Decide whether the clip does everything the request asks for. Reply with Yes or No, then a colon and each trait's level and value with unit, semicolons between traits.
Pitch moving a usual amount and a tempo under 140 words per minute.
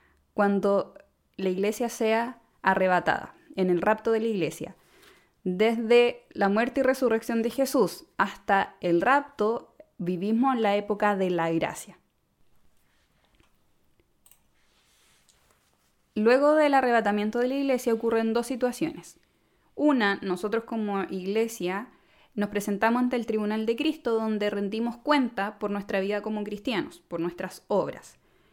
Yes: average, 3.7 semitones; slow, 125 wpm